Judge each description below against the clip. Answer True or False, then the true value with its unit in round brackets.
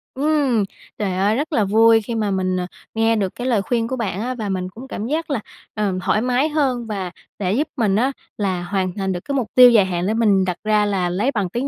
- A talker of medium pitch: False (215 Hz)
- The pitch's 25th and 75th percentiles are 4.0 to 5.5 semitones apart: True (4.4 semitones)